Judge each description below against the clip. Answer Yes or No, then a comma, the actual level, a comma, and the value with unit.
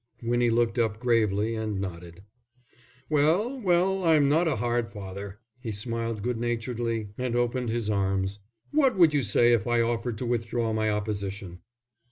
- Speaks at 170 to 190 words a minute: No, average, 160 wpm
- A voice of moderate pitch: No, low, 115 Hz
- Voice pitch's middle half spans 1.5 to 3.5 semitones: Yes, average, 2.9 semitones